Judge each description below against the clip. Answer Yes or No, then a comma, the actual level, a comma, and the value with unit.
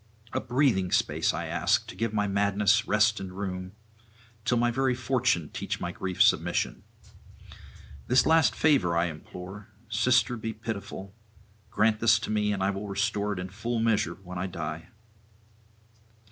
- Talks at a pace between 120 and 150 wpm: No, average, 160 wpm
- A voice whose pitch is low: Yes, low, 105 Hz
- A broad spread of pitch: No, average, 3.4 semitones